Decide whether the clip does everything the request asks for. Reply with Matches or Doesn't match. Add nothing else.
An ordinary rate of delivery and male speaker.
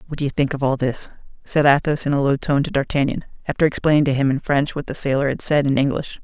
Doesn't match